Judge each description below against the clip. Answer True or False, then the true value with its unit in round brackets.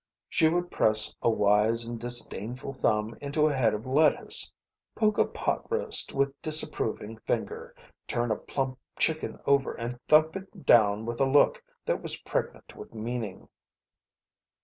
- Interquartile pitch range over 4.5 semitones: True (5.3 semitones)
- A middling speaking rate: True (150 wpm)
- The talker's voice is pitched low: True (125 Hz)